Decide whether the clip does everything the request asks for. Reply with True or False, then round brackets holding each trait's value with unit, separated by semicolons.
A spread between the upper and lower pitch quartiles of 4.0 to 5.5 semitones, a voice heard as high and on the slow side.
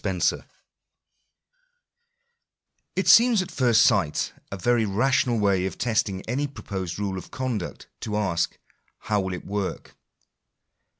False (4.3 semitones; 105 Hz; 130 wpm)